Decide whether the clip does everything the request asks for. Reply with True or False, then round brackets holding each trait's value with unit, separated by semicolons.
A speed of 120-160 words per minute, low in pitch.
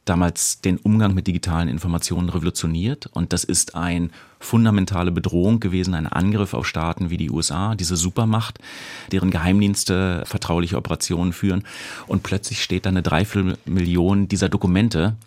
True (140 wpm; 90 Hz)